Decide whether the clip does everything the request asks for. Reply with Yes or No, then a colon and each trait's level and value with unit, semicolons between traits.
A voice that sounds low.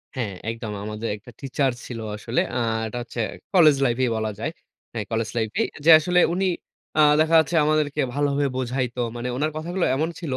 Yes: low, 130 Hz